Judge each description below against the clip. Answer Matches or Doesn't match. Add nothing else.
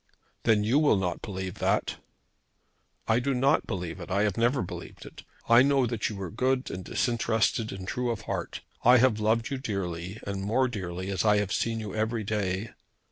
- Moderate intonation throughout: Matches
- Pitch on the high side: Doesn't match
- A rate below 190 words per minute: Doesn't match